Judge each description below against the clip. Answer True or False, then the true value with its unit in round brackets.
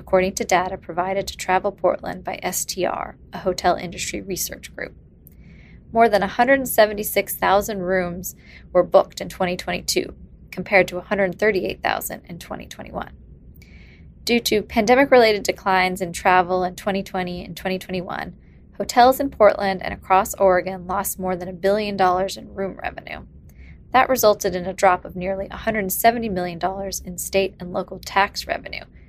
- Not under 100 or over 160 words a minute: True (140 wpm)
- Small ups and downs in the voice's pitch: True (2.0 semitones)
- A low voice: False (190 Hz)